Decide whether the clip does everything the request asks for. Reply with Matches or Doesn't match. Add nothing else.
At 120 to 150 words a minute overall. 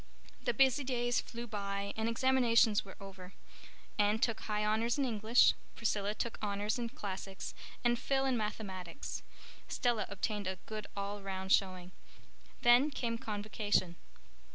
Matches